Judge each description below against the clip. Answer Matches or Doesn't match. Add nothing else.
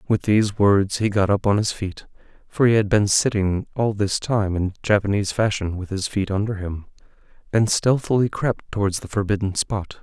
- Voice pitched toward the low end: Matches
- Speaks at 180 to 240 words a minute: Matches